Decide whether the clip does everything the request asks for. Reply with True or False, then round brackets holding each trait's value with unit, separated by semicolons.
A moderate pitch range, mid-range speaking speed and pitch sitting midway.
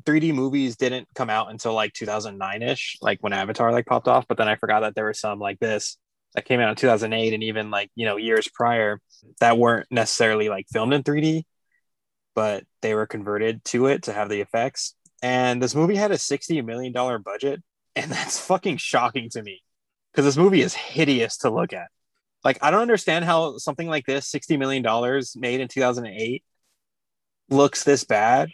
False (4.5 semitones; 195 wpm; 125 Hz)